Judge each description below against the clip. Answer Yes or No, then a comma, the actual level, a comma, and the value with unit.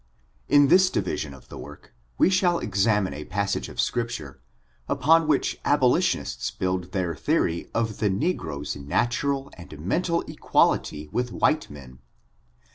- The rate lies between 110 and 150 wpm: Yes, average, 140 wpm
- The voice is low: Yes, low, 100 Hz